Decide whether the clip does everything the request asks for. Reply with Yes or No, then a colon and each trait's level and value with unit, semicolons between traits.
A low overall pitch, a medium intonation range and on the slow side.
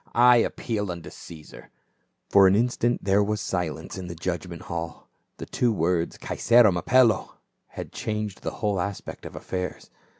No: low, 100 Hz; average, 4.0 semitones; average, 170 wpm